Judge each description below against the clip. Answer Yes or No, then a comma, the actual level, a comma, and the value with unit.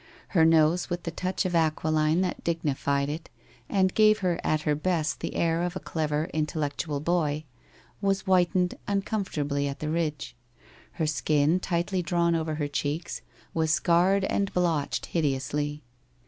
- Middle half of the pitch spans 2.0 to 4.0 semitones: Yes, average, 2.9 semitones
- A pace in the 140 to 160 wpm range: Yes, average, 155 wpm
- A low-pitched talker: No, medium, 165 Hz